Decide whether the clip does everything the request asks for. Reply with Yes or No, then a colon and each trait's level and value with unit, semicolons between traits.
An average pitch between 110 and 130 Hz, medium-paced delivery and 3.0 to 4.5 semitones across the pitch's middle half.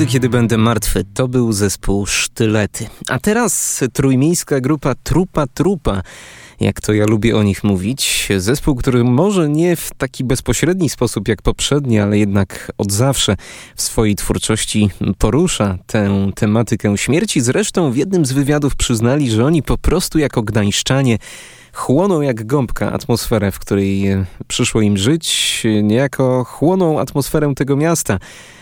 No: low, 120 Hz; average, 140 wpm; average, 5.3 semitones